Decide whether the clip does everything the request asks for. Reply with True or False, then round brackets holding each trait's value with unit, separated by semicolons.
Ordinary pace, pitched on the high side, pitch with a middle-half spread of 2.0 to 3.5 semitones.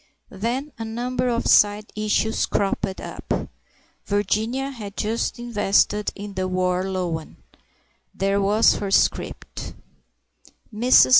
False (115 wpm; 210 Hz; 3.0 semitones)